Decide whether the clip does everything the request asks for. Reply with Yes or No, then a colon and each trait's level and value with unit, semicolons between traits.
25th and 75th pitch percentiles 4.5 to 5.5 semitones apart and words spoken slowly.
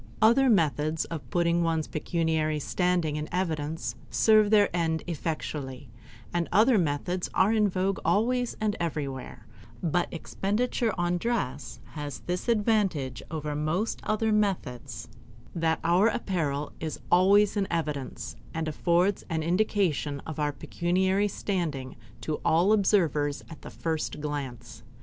Yes: average, 4.9 semitones; slow, 130 wpm